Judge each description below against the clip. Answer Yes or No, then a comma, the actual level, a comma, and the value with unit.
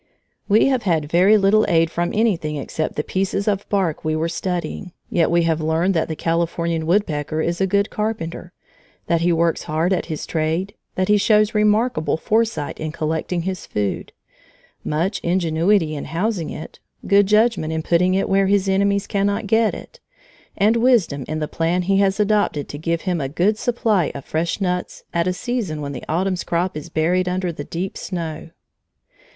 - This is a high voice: No, medium, 175 Hz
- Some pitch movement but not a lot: Yes, average, 3.9 semitones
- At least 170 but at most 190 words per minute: Yes, average, 185 wpm